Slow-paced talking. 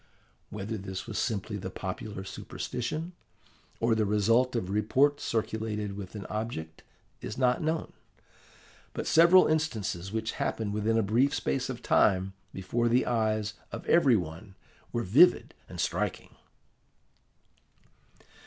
Yes: slow, 130 wpm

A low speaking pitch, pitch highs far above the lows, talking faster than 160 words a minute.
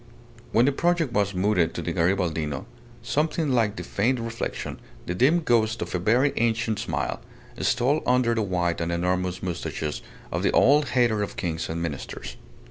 Yes: low, 105 Hz; wide, 6.1 semitones; average, 170 wpm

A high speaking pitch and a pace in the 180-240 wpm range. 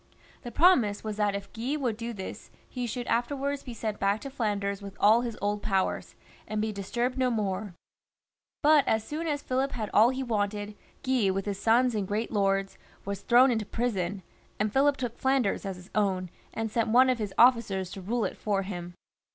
Yes: high, 220 Hz; average, 200 wpm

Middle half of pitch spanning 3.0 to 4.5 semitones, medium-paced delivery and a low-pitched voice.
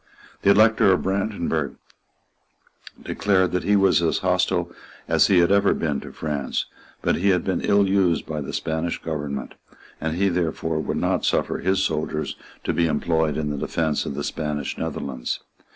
Yes: average, 3.9 semitones; average, 170 wpm; very low, 85 Hz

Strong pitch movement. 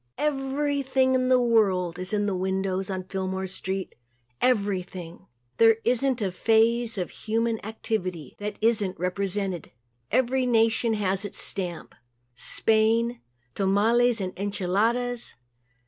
No: average, 3.8 semitones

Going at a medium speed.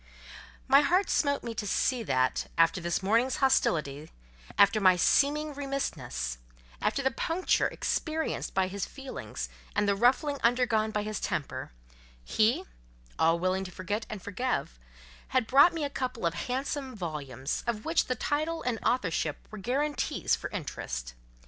Yes: average, 145 wpm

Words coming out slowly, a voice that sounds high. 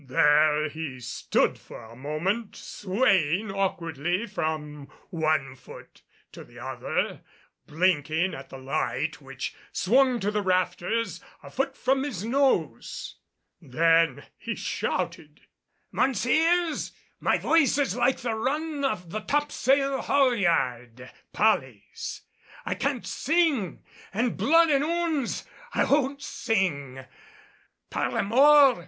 Yes: slow, 115 wpm; high, 195 Hz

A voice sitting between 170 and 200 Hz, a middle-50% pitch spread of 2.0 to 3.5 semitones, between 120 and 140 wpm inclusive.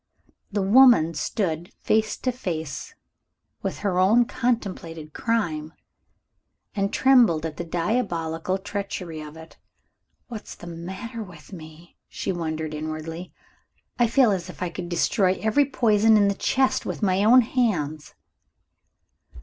No: medium, 185 Hz; average, 5.2 semitones; slow, 135 wpm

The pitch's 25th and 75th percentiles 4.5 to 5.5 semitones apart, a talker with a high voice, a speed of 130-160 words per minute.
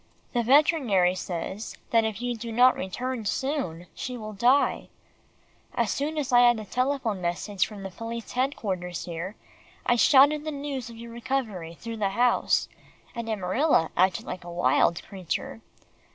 Yes: average, 5.2 semitones; high, 230 Hz; average, 155 wpm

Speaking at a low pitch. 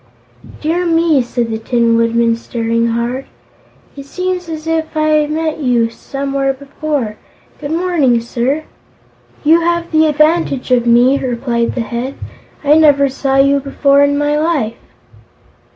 No: very high, 275 Hz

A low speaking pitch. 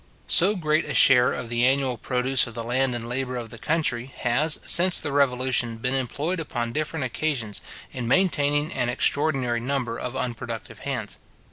Yes: low, 130 Hz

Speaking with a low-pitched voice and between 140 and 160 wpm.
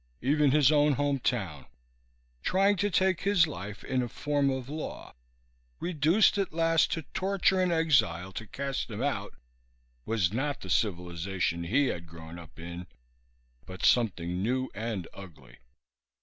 Yes: low, 130 Hz; average, 150 wpm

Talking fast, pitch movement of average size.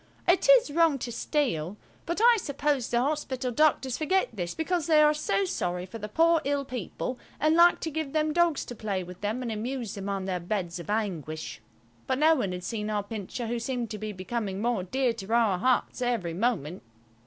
No: fast, 210 wpm; wide, 7.1 semitones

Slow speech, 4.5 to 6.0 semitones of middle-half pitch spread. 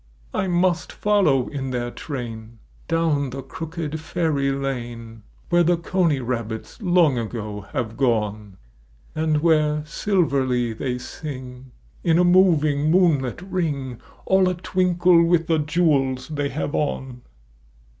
Yes: slow, 125 wpm; average, 5.1 semitones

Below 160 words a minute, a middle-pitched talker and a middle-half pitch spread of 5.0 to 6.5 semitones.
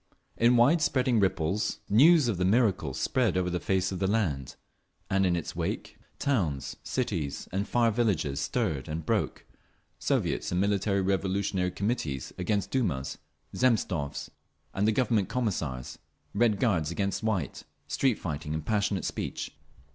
No: slow, 135 wpm; very low, 95 Hz; wide, 5.5 semitones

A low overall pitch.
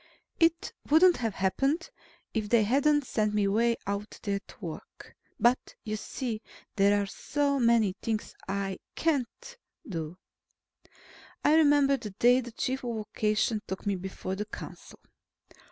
No: high, 225 Hz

